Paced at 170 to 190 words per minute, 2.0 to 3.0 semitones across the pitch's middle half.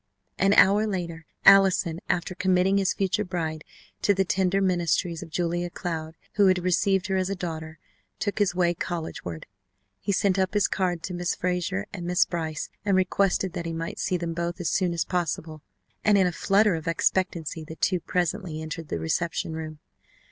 Yes: average, 185 wpm; narrow, 2.5 semitones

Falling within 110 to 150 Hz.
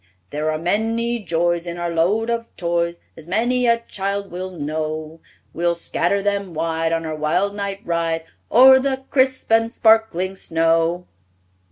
No: medium, 180 Hz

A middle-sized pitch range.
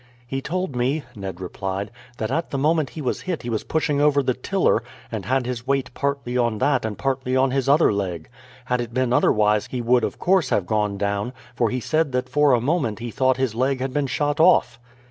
Yes: average, 3.9 semitones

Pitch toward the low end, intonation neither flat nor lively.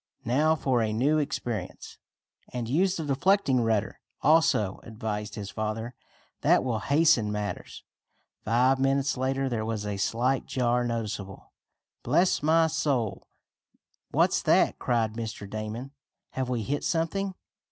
Yes: low, 125 Hz; average, 4.6 semitones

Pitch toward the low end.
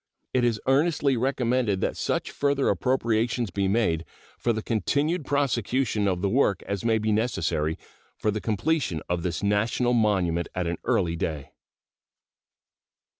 Yes: low, 110 Hz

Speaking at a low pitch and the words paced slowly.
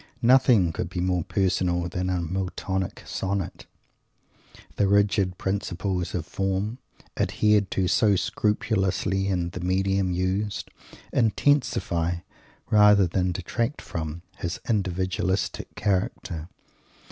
Yes: very low, 95 Hz; slow, 105 wpm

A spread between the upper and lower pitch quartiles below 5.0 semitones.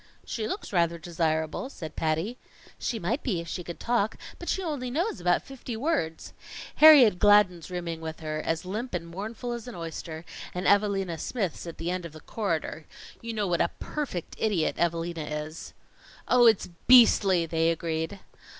No: wide, 5.6 semitones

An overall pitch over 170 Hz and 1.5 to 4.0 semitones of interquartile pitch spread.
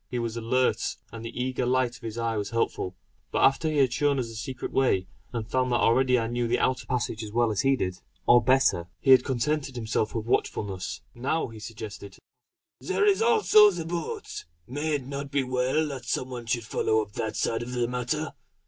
No: low, 125 Hz; average, 2.9 semitones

